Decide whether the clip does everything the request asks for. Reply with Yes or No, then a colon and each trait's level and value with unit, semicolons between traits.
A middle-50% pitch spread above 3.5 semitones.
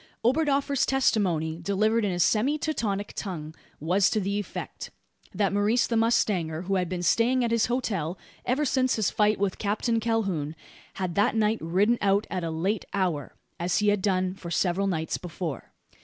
Yes: average, 4.2 semitones